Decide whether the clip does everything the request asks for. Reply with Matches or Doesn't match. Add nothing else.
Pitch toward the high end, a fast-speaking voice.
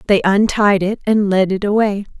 Doesn't match